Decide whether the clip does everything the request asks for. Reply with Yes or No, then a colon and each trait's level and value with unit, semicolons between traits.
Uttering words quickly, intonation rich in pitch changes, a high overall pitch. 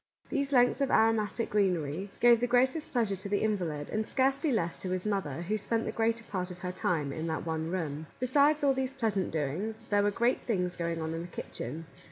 Yes: fast, 220 wpm; wide, 6.1 semitones; high, 205 Hz